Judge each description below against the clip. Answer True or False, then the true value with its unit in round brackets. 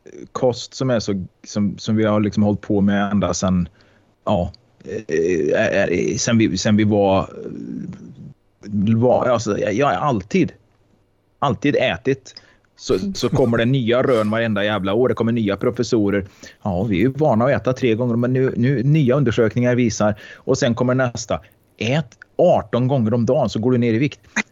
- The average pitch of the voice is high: False (115 Hz)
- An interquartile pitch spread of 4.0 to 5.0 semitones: False (3.3 semitones)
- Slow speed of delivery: False (175 wpm)